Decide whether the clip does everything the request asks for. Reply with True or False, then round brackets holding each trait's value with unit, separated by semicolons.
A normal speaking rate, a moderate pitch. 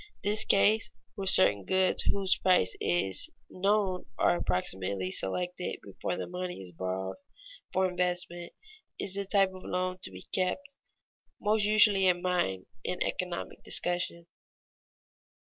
False (130 wpm; 180 Hz)